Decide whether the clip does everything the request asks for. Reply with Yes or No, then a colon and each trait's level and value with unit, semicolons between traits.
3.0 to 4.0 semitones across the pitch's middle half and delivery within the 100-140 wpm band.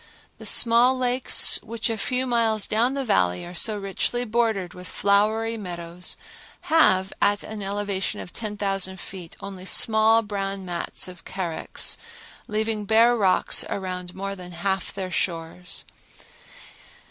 Yes: average, 3.4 semitones; slow, 135 wpm